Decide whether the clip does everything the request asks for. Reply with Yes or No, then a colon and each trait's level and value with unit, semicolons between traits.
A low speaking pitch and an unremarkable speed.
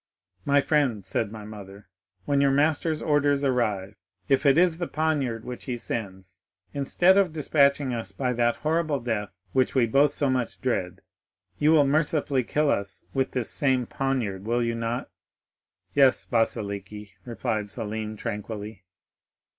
Yes: low, 125 Hz; average, 145 wpm